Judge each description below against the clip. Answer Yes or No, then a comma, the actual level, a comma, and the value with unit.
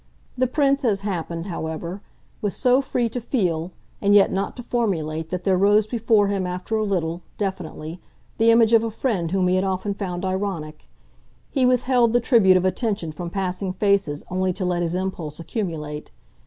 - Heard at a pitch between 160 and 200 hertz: Yes, high, 190 Hz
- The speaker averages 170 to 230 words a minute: Yes, average, 180 wpm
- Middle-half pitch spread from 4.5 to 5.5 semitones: No, average, 4.1 semitones